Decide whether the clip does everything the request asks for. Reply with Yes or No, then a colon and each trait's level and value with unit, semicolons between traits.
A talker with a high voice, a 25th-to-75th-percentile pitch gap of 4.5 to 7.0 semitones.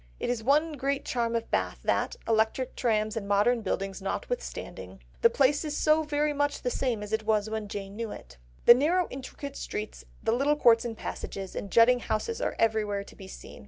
Yes: high, 230 Hz; average, 4.8 semitones